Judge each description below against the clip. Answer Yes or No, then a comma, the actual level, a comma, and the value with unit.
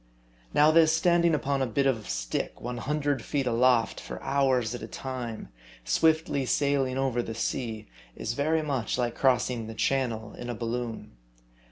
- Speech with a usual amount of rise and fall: Yes, average, 3.4 semitones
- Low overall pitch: Yes, low, 130 Hz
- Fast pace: No, average, 160 wpm